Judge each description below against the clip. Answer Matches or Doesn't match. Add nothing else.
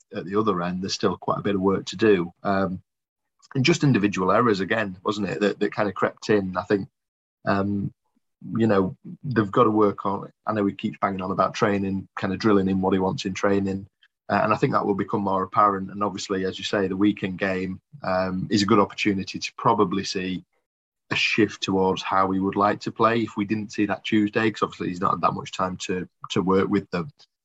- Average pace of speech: Doesn't match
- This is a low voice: Matches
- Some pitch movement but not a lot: Doesn't match